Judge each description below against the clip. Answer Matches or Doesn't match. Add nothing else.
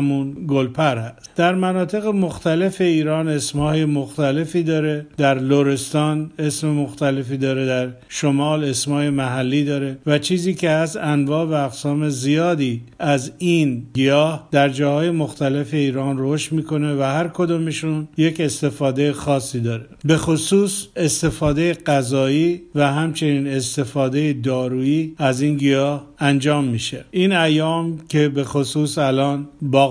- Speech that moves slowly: Doesn't match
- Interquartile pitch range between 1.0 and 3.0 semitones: Matches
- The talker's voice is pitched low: Doesn't match